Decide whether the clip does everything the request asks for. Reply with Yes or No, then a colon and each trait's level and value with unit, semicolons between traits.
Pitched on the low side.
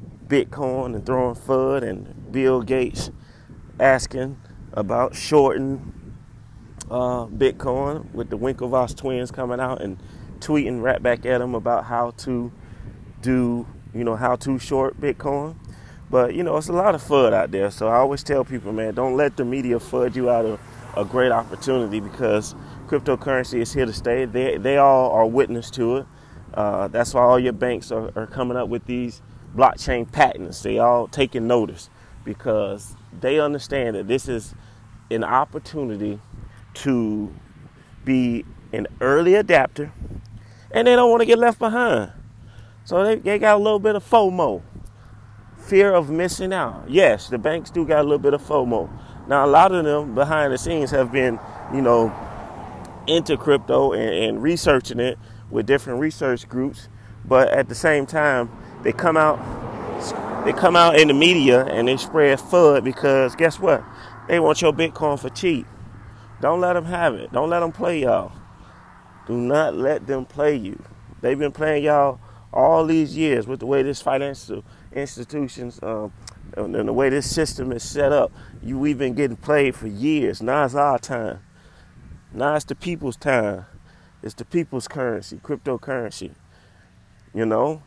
Yes: low, 125 Hz